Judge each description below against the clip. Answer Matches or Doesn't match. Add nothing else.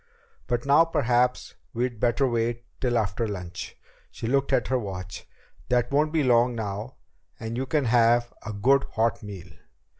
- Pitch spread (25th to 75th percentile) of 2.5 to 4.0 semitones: Matches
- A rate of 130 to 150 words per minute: Doesn't match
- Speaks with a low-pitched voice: Matches